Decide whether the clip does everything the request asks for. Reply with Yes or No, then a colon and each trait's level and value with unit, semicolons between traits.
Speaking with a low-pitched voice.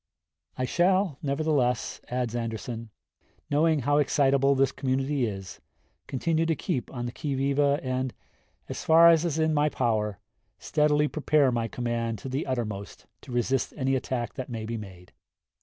Yes: low, 130 Hz